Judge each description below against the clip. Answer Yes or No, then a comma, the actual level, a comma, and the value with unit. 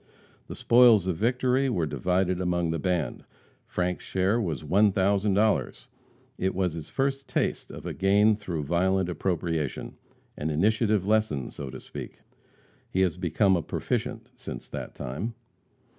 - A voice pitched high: No, very low, 95 Hz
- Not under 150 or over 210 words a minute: No, average, 140 wpm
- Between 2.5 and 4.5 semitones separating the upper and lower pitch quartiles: Yes, average, 3.8 semitones